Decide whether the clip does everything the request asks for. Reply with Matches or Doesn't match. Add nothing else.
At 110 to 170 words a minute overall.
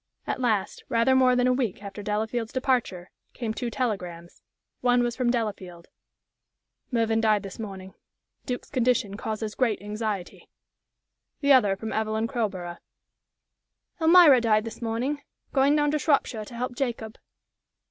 Matches